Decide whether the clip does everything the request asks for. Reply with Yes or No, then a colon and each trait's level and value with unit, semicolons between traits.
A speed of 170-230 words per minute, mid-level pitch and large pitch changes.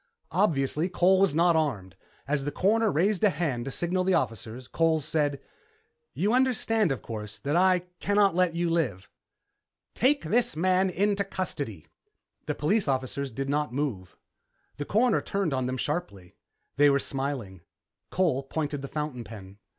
No: average, 160 wpm; medium, 150 Hz; wide, 5.8 semitones